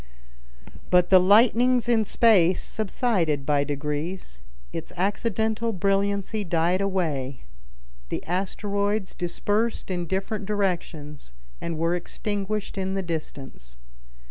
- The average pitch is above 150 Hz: Yes, high, 190 Hz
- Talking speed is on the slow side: Yes, slow, 105 wpm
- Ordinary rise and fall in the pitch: Yes, average, 3.8 semitones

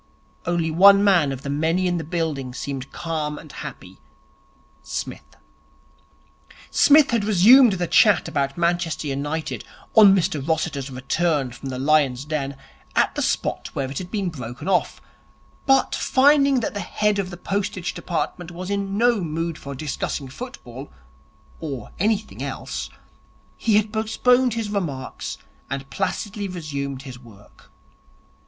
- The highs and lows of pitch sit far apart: Yes, wide, 6.5 semitones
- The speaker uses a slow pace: No, average, 145 wpm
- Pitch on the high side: No, medium, 170 Hz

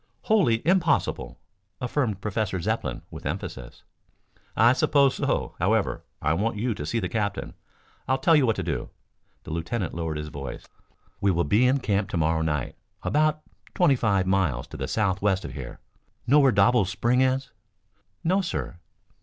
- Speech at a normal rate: Yes, average, 165 wpm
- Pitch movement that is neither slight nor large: No, wide, 7.2 semitones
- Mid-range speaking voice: No, low, 105 Hz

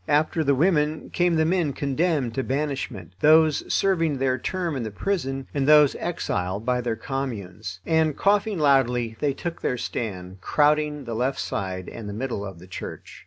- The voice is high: No, low, 135 Hz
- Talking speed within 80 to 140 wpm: No, average, 175 wpm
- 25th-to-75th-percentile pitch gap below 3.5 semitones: No, wide, 5.5 semitones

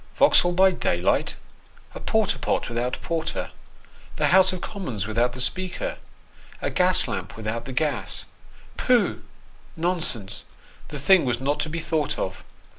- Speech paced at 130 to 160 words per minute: Yes, average, 150 wpm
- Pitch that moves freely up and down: Yes, wide, 7.2 semitones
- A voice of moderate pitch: Yes, medium, 150 Hz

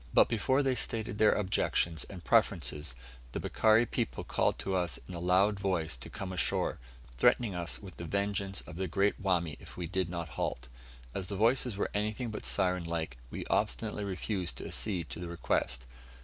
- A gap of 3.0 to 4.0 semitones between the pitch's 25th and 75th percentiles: Yes, average, 3.5 semitones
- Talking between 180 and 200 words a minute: Yes, average, 190 wpm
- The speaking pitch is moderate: No, very low, 95 Hz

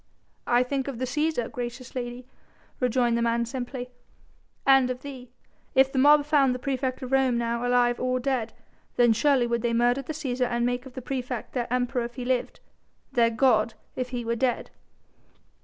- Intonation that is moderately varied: No, narrow, 1.7 semitones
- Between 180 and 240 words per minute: Yes, average, 190 wpm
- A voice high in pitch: Yes, very high, 250 Hz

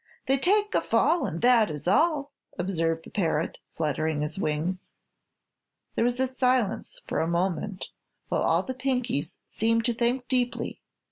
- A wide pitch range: Yes, wide, 7.6 semitones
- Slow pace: No, average, 150 wpm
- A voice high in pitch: Yes, high, 220 Hz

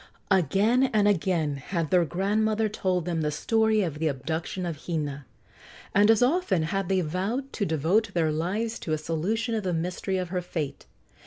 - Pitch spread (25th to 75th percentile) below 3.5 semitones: No, average, 4.9 semitones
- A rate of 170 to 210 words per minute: Yes, average, 180 wpm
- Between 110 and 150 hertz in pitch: No, medium, 185 Hz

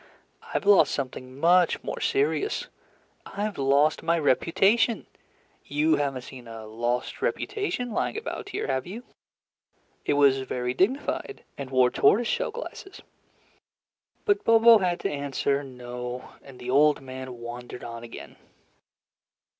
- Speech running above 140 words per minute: No, slow, 135 wpm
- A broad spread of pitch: Yes, wide, 8.5 semitones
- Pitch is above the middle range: No, medium, 140 Hz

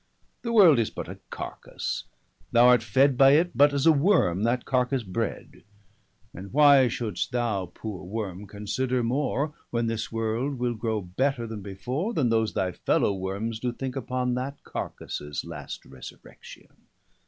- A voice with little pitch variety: No, average, 4.2 semitones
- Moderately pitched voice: No, low, 120 Hz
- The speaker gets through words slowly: No, average, 165 wpm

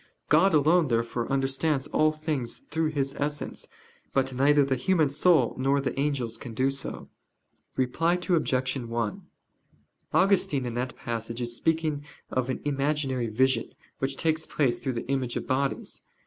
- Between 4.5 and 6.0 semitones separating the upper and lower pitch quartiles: No, average, 3.3 semitones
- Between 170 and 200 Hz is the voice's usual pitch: No, low, 135 Hz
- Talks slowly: No, average, 150 wpm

